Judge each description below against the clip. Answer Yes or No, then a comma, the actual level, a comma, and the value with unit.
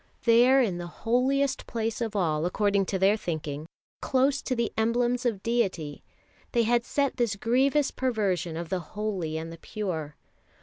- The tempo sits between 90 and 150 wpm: No, average, 165 wpm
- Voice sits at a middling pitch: No, high, 215 Hz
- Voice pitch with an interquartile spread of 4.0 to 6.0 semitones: Yes, wide, 5.6 semitones